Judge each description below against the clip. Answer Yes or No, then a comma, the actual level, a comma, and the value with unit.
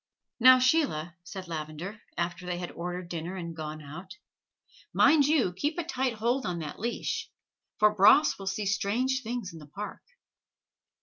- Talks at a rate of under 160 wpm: No, average, 165 wpm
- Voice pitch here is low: No, high, 190 Hz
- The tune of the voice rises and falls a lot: Yes, wide, 6.5 semitones